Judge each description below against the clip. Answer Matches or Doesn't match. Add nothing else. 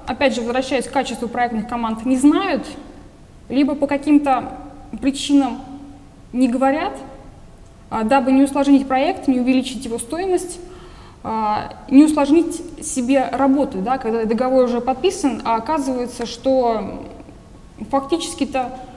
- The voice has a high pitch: Matches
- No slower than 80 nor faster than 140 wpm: Matches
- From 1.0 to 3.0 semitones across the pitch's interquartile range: Matches